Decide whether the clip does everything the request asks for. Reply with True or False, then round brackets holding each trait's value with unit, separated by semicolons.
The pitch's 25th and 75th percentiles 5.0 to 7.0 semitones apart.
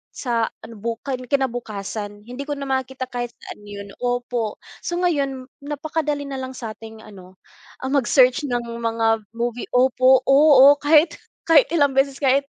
False (3.4 semitones)